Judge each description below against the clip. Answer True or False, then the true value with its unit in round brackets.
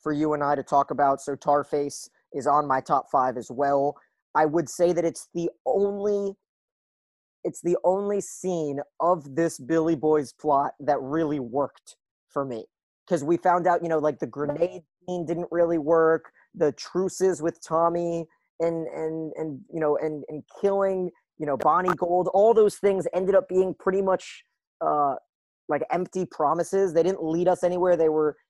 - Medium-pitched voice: True (165 Hz)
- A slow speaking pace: False (180 wpm)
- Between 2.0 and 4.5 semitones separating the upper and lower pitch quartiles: True (3.4 semitones)